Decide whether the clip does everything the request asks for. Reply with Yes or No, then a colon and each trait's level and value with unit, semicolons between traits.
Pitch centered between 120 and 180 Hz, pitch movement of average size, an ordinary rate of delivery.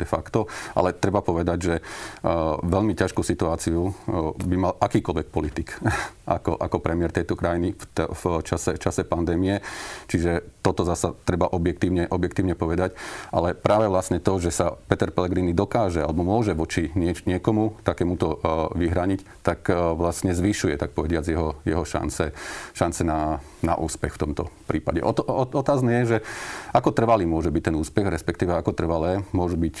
No: very low, 90 Hz; average, 3.2 semitones; average, 155 wpm